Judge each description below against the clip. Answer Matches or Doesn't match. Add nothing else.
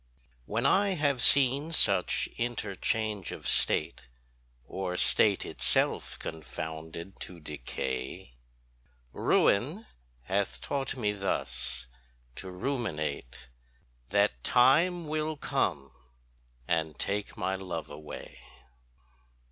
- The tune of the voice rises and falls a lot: Matches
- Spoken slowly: Matches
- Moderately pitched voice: Doesn't match